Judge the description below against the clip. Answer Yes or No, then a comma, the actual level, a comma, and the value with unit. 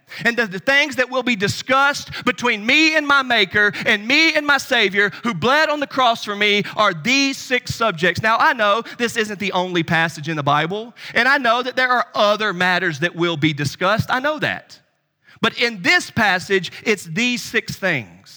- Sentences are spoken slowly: No, fast, 205 wpm